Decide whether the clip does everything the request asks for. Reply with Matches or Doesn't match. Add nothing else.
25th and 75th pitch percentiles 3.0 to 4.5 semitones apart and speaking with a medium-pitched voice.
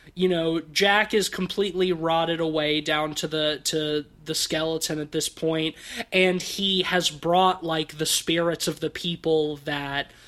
Doesn't match